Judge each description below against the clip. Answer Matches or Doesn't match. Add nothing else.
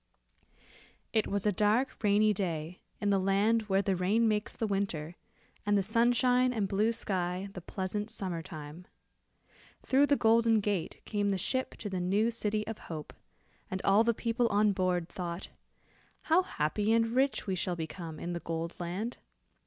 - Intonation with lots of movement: Doesn't match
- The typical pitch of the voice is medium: Doesn't match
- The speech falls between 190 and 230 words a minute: Doesn't match